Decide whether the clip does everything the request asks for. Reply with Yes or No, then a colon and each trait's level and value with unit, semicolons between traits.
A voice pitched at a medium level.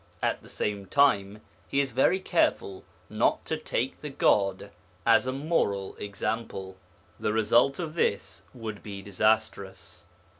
No: low, 110 Hz